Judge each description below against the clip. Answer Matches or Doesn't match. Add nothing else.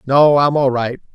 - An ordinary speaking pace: Doesn't match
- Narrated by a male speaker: Matches